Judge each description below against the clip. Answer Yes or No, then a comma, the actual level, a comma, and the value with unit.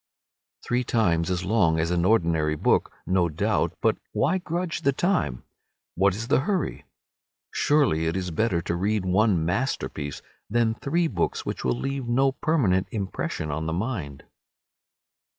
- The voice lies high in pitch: No, very low, 95 Hz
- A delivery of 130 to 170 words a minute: Yes, average, 150 wpm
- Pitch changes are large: Yes, wide, 7.6 semitones